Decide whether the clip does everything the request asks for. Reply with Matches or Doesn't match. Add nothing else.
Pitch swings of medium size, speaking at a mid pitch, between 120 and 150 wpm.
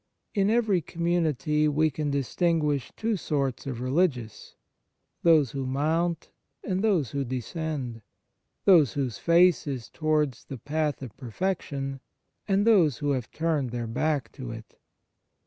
Matches